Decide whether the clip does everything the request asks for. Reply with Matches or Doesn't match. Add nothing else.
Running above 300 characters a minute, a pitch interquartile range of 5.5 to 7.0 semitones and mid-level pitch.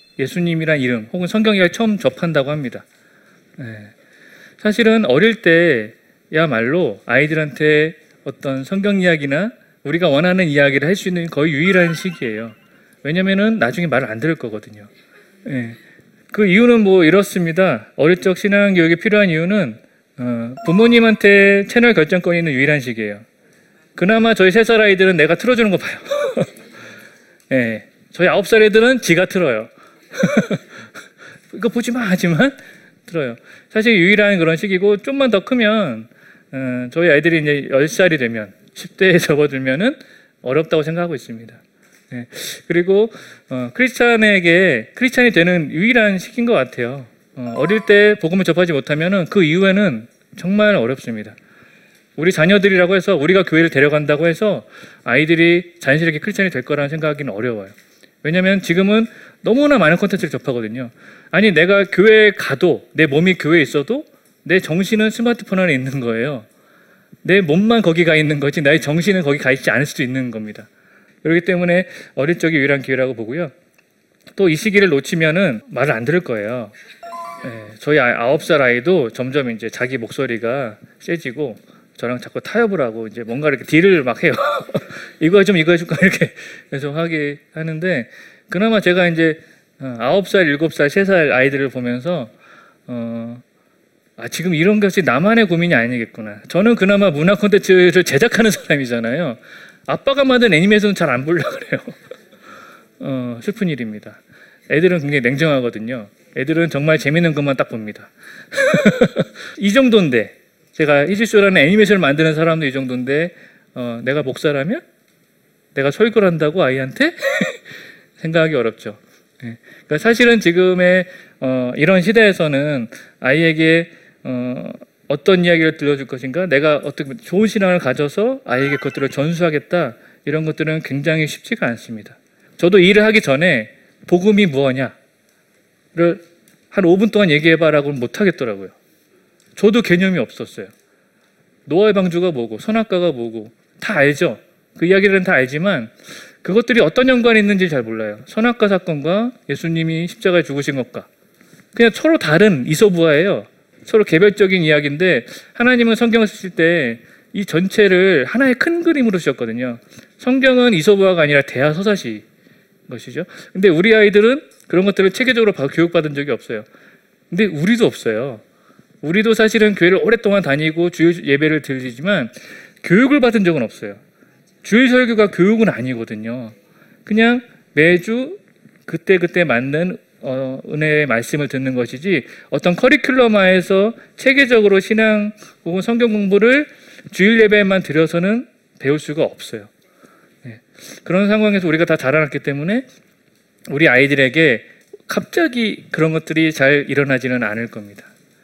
Matches